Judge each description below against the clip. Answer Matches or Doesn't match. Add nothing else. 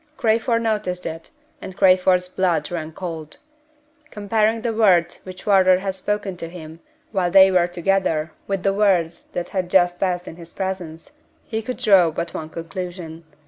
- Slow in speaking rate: Doesn't match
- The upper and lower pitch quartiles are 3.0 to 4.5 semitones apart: Doesn't match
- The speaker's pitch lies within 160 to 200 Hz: Matches